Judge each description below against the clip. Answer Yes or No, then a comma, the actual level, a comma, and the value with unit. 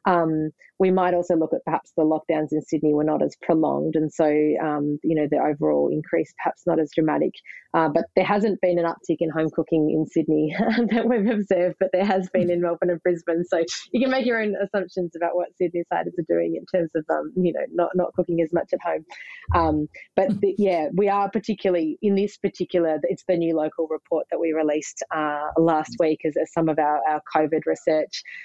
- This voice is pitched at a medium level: Yes, medium, 170 Hz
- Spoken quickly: Yes, fast, 220 wpm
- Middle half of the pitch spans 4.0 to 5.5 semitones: No, average, 3.2 semitones